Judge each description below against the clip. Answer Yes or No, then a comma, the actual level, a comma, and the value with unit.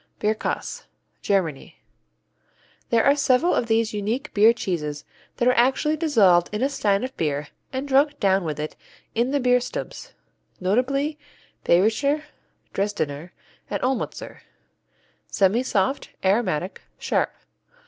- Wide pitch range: Yes, wide, 6.0 semitones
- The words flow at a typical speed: No, slow, 115 wpm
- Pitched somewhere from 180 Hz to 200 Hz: No, high, 225 Hz